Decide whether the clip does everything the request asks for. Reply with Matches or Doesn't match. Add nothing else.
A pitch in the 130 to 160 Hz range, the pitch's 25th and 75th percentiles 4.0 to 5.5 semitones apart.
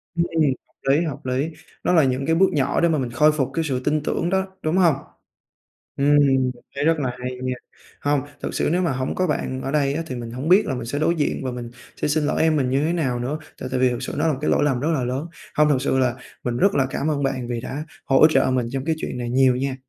Doesn't match